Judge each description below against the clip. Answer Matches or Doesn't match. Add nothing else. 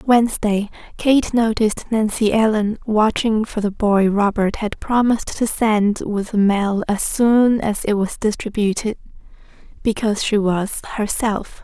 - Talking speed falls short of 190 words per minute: Matches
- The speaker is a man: Doesn't match